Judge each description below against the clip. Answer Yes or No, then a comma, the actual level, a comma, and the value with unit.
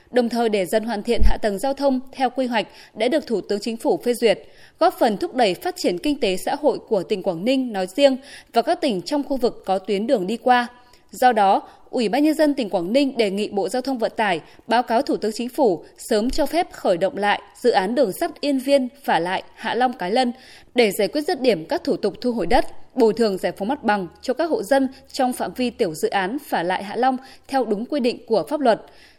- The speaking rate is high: Yes, fast, 260 wpm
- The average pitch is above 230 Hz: Yes, high, 245 Hz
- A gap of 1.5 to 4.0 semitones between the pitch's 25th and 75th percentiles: No, average, 4.4 semitones